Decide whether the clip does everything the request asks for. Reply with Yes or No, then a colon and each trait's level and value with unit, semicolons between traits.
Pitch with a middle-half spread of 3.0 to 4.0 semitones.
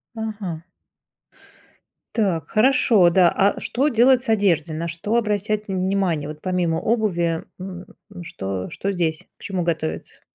No: average, 4.4 semitones